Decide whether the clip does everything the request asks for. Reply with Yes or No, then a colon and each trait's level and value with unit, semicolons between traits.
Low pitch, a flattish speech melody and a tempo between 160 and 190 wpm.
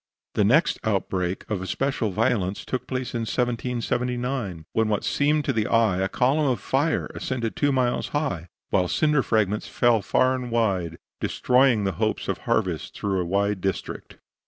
No: low, 115 Hz; average, 4.7 semitones; average, 165 wpm